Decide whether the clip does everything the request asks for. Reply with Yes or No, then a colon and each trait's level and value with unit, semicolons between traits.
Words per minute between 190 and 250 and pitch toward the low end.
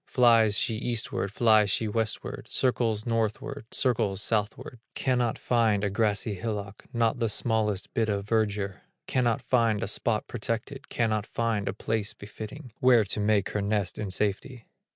No: average, 150 wpm; low, 110 Hz